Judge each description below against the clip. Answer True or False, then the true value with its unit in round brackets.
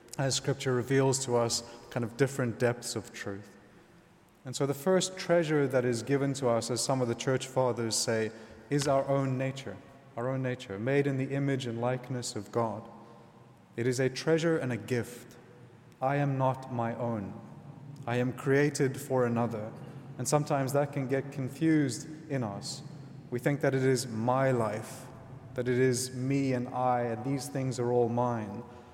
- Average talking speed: True (180 wpm)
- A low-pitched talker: True (130 Hz)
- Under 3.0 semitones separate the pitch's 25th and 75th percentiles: True (2.6 semitones)